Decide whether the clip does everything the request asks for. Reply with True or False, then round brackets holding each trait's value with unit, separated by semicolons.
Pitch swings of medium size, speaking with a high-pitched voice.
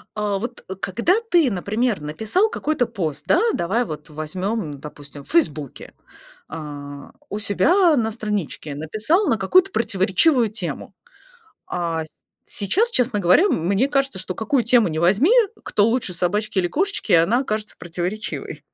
False (6.3 semitones; 210 Hz)